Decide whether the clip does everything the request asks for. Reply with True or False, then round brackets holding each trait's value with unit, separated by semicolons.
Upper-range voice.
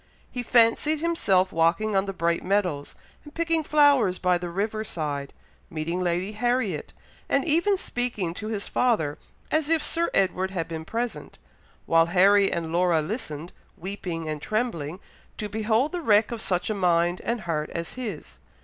True (195 Hz)